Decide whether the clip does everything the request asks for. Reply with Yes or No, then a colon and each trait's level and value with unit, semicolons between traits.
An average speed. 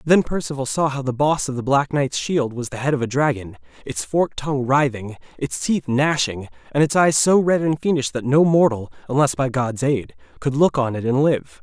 No: fast, 225 wpm